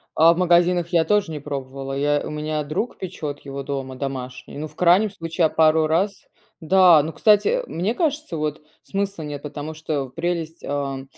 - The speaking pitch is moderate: Yes, medium, 160 Hz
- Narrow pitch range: No, average, 3.7 semitones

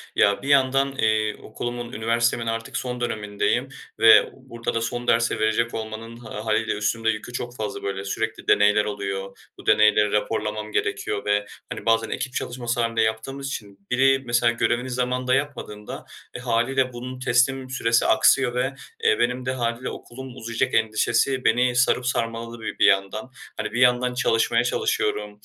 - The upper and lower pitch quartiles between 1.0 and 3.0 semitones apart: Yes, narrow, 2.5 semitones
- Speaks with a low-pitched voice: Yes, low, 115 Hz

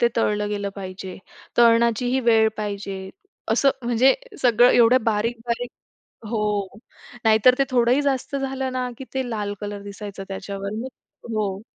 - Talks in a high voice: Yes, high, 230 Hz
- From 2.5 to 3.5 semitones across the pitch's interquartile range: Yes, average, 3.2 semitones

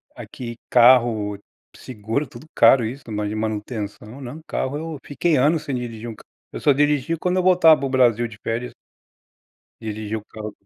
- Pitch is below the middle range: Yes, low, 125 Hz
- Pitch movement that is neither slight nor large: Yes, average, 5.0 semitones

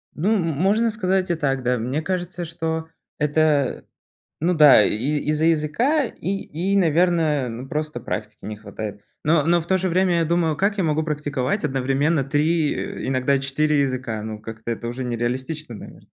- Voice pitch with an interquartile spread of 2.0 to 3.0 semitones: No, average, 4.8 semitones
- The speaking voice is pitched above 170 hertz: No, medium, 150 Hz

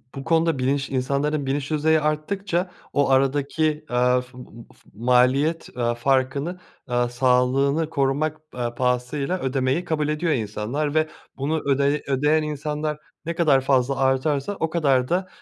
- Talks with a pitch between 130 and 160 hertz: Yes, medium, 140 Hz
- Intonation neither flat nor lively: Yes, average, 3.0 semitones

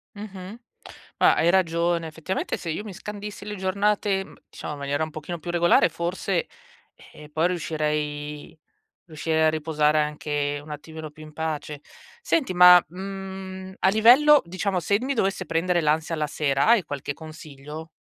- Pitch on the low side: No, medium, 170 Hz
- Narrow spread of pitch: No, average, 3.9 semitones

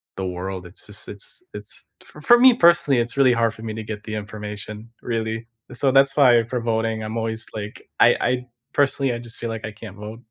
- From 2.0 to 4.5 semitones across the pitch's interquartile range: Yes, average, 2.9 semitones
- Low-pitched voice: Yes, low, 115 Hz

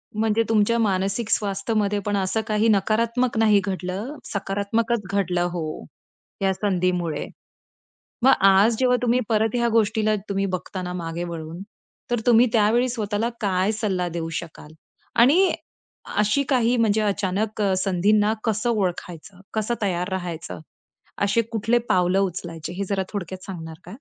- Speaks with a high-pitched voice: Yes, high, 205 Hz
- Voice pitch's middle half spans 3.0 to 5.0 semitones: Yes, average, 3.4 semitones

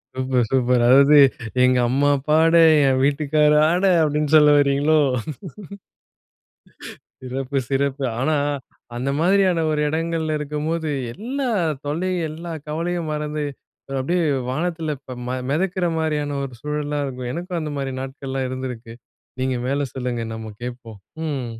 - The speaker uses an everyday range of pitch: Yes, average, 3.3 semitones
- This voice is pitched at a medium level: Yes, medium, 145 Hz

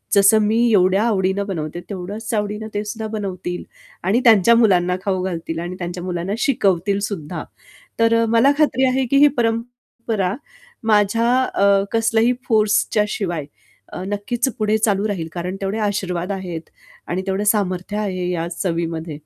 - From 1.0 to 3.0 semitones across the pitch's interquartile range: No, average, 3.5 semitones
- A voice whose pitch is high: Yes, high, 200 Hz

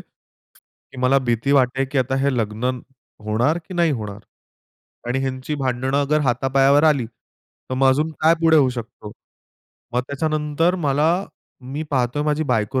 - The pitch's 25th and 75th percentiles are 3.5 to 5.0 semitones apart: No, average, 3.1 semitones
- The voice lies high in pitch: No, low, 135 Hz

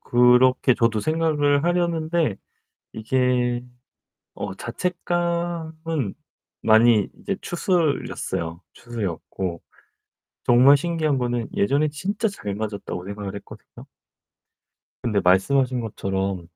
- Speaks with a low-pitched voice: Yes, low, 125 Hz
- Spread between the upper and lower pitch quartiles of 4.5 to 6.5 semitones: No, wide, 7.5 semitones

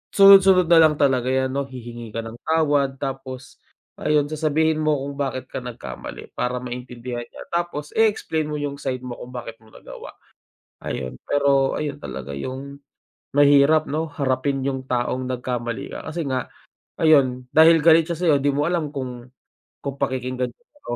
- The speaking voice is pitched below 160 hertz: Yes, medium, 140 Hz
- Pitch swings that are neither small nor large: Yes, average, 3.4 semitones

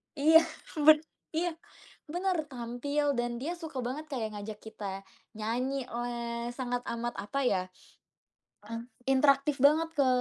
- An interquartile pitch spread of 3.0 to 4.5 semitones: Yes, average, 4.0 semitones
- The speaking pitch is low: No, very high, 260 Hz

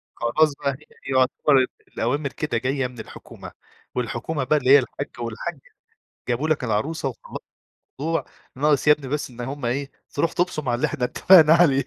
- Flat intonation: No, average, 3.2 semitones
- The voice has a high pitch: No, medium, 140 Hz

